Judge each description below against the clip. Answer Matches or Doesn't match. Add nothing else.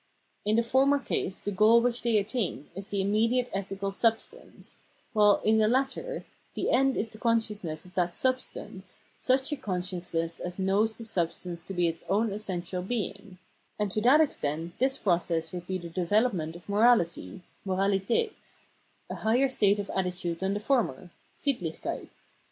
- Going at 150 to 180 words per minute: Matches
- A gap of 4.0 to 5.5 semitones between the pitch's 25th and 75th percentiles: Matches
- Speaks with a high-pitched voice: Matches